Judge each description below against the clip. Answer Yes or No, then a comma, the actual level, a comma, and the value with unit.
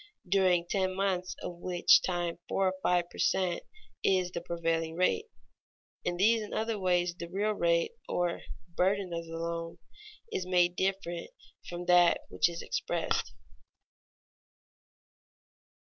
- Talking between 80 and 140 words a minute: Yes, slow, 135 wpm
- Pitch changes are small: Yes, narrow, 1.8 semitones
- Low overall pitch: No, medium, 180 Hz